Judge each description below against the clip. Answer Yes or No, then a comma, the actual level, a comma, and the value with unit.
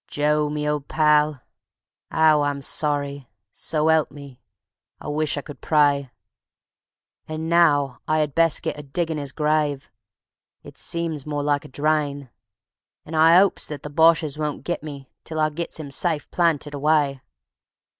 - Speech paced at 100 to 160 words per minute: Yes, average, 155 wpm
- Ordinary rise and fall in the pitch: No, narrow, 1.7 semitones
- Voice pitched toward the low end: No, medium, 150 Hz